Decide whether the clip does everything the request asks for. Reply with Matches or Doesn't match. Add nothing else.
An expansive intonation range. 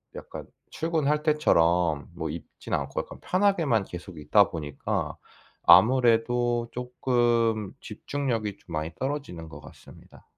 Matches